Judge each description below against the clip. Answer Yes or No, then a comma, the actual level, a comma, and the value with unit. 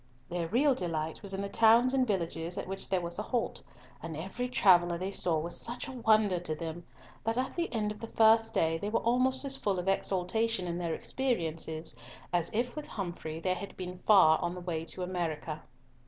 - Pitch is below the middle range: No, medium, 185 Hz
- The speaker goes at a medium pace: No, fast, 215 wpm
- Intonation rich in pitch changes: No, average, 5.0 semitones